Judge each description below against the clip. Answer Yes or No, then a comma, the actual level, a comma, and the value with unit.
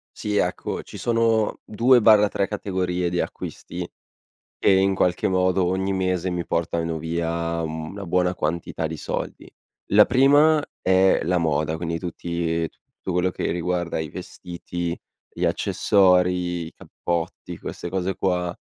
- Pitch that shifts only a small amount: Yes, narrow, 2.3 semitones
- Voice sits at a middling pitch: No, very low, 90 Hz